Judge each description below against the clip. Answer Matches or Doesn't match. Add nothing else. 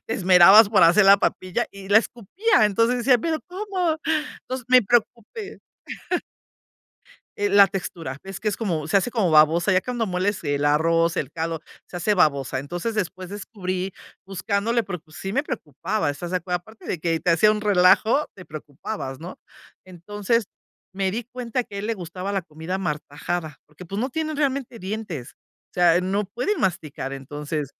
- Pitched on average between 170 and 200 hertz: Matches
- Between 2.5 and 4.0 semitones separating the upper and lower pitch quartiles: Doesn't match